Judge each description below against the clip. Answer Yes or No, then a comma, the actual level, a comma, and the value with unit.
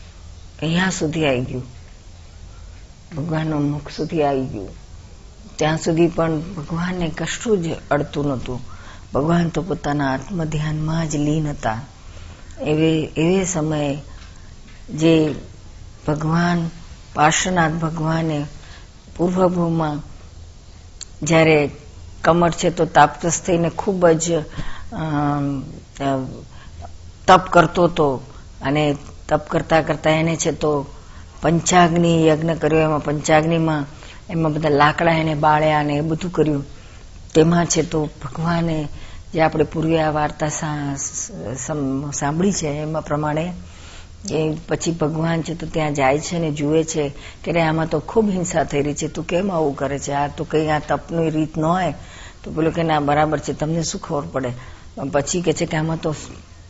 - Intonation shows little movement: No, average, 3.3 semitones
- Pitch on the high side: No, medium, 150 Hz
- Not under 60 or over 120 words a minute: No, average, 130 wpm